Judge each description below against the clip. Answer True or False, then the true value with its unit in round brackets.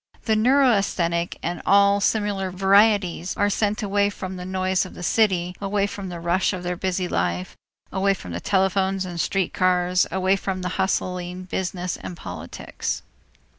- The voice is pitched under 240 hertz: True (185 Hz)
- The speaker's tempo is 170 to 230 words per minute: False (160 wpm)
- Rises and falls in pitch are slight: True (1.9 semitones)